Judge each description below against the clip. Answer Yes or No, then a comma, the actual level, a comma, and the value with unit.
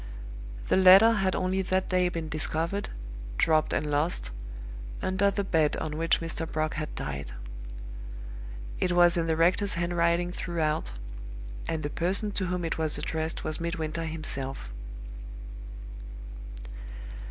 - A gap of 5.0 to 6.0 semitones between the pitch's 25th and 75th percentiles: No, average, 2.8 semitones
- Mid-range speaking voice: Yes, medium, 165 Hz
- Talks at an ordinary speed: No, slow, 130 wpm